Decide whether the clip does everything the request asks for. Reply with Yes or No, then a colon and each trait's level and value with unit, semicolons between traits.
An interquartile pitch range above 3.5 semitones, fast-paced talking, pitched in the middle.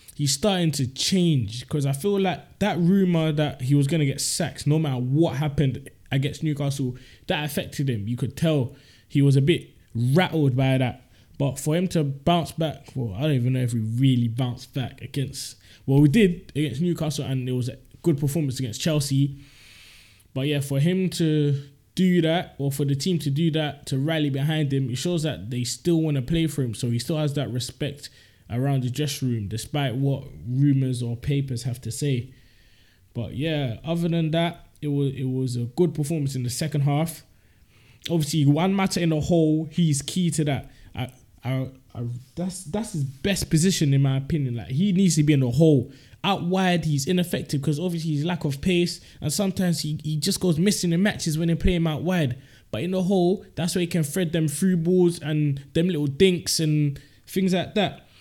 Yes: average, 4.2 semitones; fast, 210 wpm; medium, 145 Hz